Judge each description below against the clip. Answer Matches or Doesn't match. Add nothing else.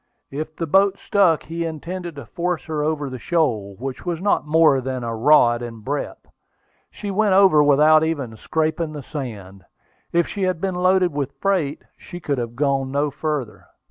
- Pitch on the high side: Doesn't match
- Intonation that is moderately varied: Matches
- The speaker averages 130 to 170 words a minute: Doesn't match